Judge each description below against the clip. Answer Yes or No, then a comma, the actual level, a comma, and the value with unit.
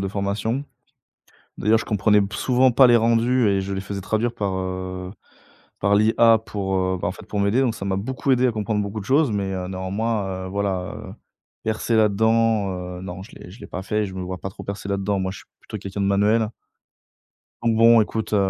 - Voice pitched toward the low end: Yes, low, 100 Hz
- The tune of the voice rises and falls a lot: No, average, 2.8 semitones